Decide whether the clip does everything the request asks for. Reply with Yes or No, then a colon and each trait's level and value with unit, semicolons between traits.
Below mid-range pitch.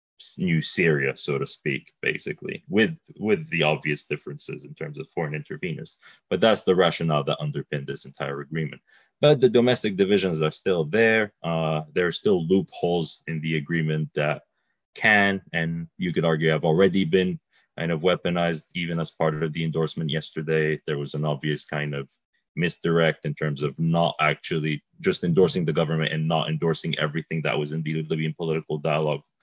Yes: very low, 80 Hz